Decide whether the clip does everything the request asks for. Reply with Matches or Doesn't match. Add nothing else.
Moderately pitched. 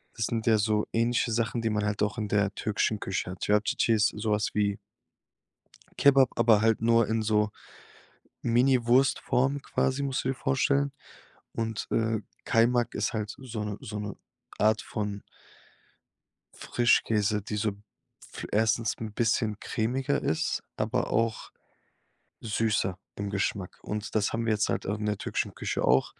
Doesn't match